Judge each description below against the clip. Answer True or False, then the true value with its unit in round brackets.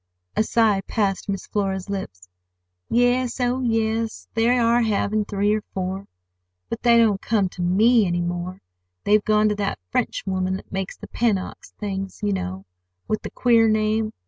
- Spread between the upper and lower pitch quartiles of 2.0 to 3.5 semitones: True (2.9 semitones)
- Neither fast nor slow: True (170 wpm)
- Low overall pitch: False (210 Hz)